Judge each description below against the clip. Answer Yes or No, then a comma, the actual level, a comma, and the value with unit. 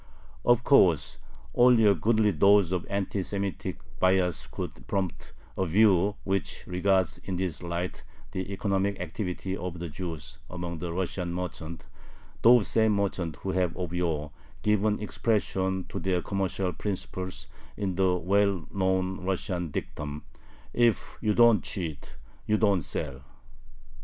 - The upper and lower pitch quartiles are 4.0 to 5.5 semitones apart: No, narrow, 2.4 semitones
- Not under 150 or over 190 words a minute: No, slow, 135 wpm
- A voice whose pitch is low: Yes, very low, 95 Hz